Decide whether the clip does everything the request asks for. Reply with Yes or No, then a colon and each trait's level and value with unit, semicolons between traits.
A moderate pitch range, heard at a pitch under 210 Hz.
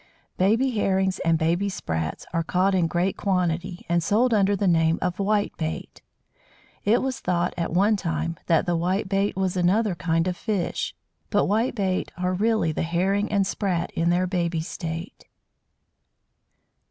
Yes: average, 3.0 semitones; medium, 185 Hz